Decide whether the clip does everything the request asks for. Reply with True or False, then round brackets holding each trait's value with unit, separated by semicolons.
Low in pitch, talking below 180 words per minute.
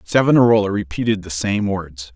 True (100 Hz; 140 wpm)